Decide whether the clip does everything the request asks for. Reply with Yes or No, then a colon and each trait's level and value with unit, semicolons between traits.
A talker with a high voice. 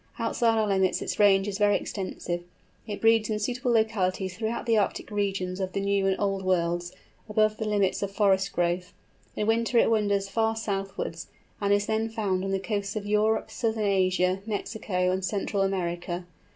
Yes: high, 200 Hz